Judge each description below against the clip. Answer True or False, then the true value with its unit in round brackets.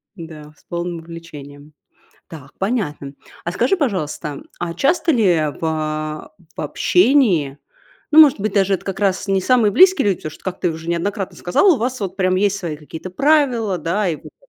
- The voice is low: False (185 Hz)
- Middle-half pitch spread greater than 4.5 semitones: True (5.2 semitones)